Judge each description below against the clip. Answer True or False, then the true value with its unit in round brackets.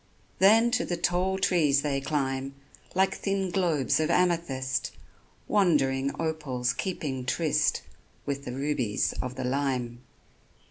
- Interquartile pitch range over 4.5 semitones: True (5.1 semitones)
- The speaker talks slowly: True (125 wpm)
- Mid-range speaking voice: True (145 Hz)